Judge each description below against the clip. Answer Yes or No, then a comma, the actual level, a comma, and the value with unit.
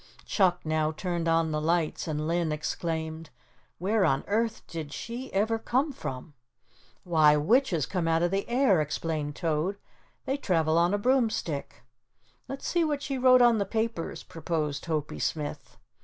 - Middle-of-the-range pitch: Yes, medium, 170 Hz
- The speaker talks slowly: No, average, 155 wpm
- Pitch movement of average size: No, wide, 6.1 semitones